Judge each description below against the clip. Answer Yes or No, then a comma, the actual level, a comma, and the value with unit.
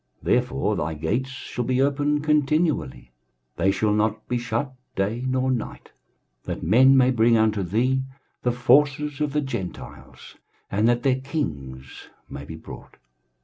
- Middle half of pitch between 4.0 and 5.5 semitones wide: Yes, average, 4.6 semitones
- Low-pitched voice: Yes, low, 125 Hz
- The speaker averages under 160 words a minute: Yes, average, 150 wpm